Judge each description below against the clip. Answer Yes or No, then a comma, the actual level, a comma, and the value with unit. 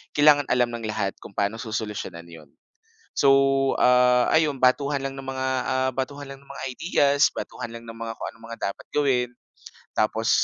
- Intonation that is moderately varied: Yes, average, 3.3 semitones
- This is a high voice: No, low, 125 Hz